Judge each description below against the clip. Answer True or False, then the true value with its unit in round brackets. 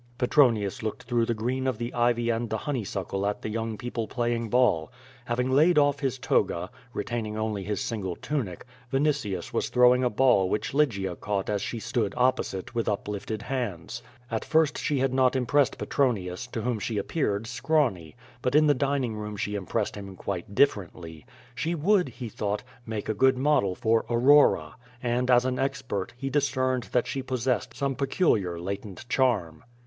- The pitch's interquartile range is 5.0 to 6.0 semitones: False (4.3 semitones)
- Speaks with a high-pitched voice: False (120 Hz)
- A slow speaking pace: False (180 wpm)